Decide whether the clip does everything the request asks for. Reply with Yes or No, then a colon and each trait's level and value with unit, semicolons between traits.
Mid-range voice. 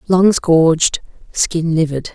Yes: medium, 165 Hz